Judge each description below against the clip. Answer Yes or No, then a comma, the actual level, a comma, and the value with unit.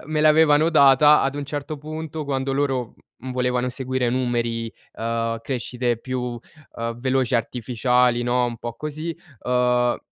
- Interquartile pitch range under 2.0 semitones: No, average, 2.8 semitones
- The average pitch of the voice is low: Yes, low, 125 Hz